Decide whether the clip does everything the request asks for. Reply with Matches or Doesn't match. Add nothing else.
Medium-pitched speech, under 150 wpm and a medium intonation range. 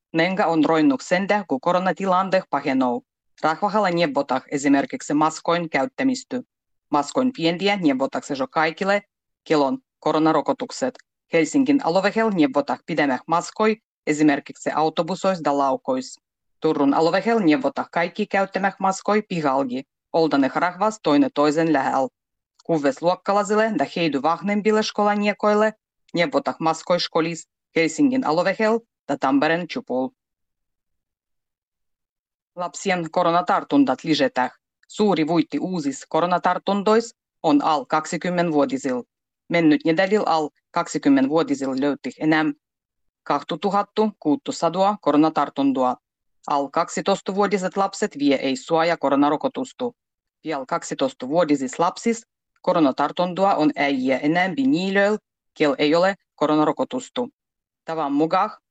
Doesn't match